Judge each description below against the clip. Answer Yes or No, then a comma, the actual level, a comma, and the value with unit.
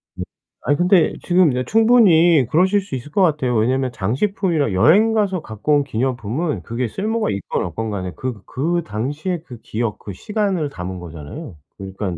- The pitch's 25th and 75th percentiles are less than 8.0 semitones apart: No, wide, 8.5 semitones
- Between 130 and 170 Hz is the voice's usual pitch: Yes, medium, 140 Hz